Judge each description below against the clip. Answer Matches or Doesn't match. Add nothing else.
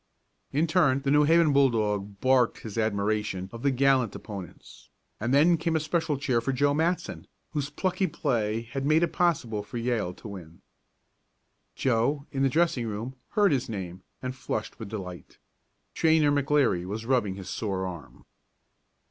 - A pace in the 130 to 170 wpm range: Matches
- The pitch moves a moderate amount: Doesn't match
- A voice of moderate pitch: Doesn't match